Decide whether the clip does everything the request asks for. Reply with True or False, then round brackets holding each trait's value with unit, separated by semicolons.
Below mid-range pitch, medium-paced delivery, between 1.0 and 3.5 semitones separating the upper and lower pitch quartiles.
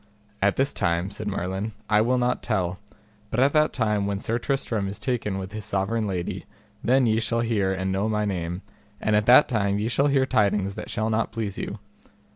False (105 Hz; 210 wpm; 3.1 semitones)